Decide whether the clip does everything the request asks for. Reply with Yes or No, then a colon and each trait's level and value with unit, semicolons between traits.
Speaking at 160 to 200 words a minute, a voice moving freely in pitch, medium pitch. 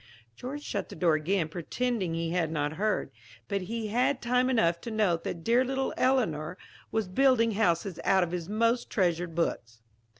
No: average, 185 wpm; wide, 6.0 semitones; high, 195 Hz